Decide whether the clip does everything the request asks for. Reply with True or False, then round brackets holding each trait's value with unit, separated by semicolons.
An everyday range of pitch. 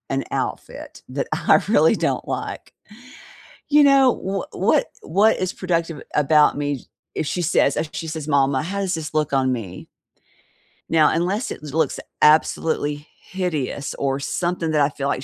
True (3.8 semitones)